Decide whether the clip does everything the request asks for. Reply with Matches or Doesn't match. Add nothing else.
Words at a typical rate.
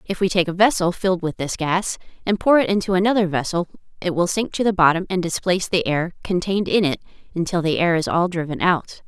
Doesn't match